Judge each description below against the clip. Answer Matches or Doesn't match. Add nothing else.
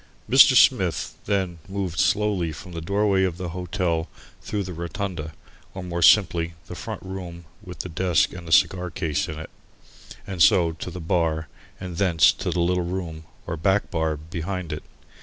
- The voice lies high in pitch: Doesn't match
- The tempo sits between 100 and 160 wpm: Doesn't match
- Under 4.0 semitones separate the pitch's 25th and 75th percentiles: Matches